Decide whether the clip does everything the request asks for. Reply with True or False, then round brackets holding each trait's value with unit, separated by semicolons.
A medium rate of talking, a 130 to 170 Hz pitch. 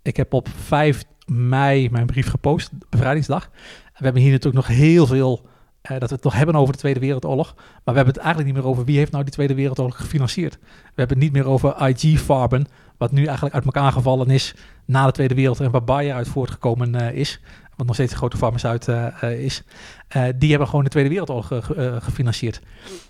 False (215 wpm; 135 Hz)